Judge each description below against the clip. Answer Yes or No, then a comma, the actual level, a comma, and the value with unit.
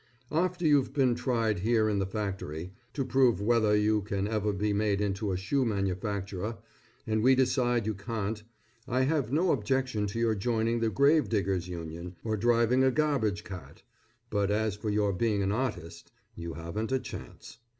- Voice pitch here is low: Yes, low, 110 Hz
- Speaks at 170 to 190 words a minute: Yes, average, 175 wpm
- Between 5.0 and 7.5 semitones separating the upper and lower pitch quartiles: No, average, 3.7 semitones